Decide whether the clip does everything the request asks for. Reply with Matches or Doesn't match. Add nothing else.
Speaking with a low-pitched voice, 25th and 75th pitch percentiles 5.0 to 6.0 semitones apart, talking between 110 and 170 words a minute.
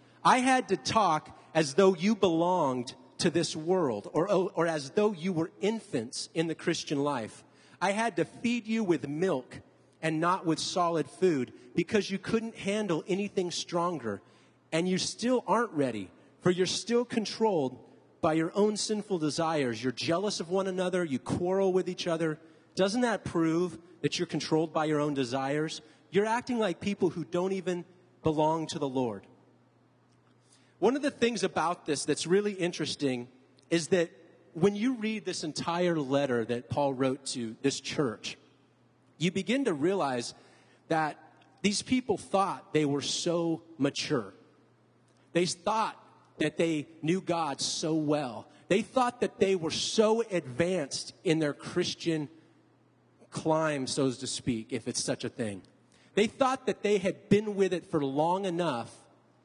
Doesn't match